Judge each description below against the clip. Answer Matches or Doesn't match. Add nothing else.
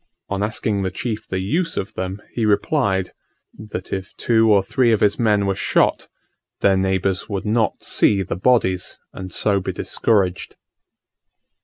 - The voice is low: Matches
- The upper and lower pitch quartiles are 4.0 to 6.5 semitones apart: Doesn't match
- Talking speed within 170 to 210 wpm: Doesn't match